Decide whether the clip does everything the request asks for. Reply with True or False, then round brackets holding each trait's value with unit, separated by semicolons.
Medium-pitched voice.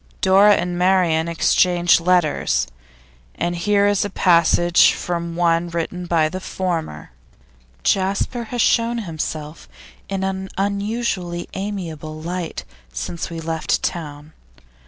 True (175 Hz)